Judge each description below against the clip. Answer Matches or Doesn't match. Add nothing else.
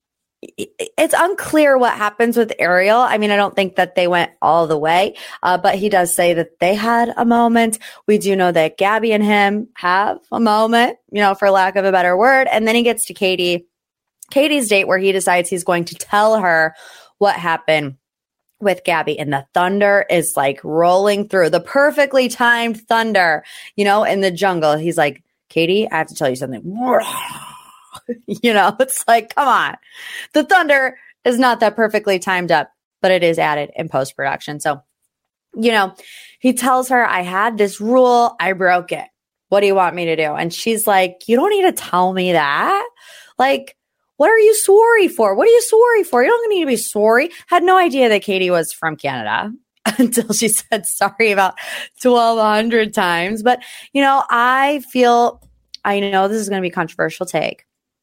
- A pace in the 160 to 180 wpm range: Doesn't match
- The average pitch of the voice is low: Doesn't match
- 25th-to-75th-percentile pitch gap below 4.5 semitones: Doesn't match